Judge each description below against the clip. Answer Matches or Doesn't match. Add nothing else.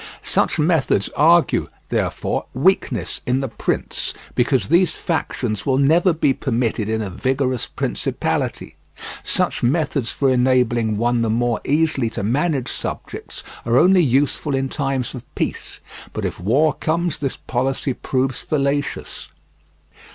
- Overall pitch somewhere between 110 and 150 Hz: Matches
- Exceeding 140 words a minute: Doesn't match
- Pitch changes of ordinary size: Matches